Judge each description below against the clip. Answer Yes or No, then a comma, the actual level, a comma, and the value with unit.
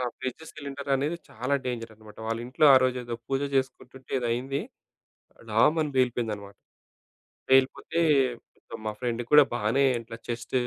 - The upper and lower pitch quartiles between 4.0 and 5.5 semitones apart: No, average, 2.7 semitones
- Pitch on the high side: No, low, 125 Hz